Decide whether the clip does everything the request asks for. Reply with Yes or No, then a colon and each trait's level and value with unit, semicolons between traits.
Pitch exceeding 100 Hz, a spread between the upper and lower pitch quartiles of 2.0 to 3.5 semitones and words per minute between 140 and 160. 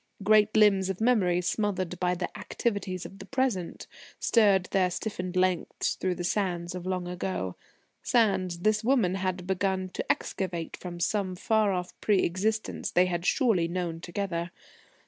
Yes: medium, 185 Hz; narrow, 2.6 semitones; average, 155 wpm